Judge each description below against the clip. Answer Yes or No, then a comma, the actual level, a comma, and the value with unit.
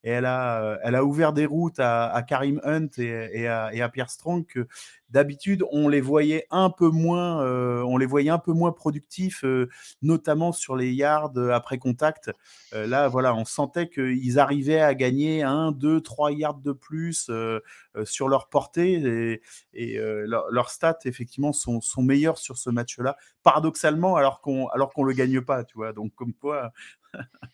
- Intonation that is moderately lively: Yes, average, 3.9 semitones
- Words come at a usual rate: Yes, average, 190 wpm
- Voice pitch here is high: No, low, 135 Hz